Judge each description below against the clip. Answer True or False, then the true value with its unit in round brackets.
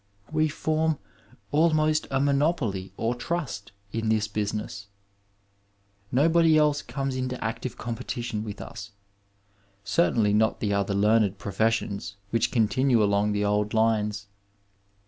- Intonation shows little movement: False (5.2 semitones)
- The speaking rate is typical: False (125 wpm)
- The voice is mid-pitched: False (115 Hz)